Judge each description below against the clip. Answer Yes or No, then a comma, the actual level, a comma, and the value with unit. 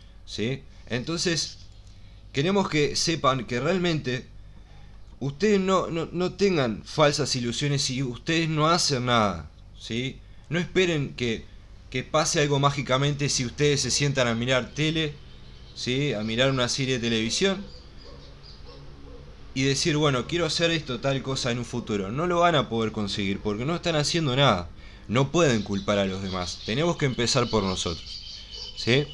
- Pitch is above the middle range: No, low, 125 Hz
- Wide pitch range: Yes, wide, 7.0 semitones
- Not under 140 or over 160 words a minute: Yes, average, 155 wpm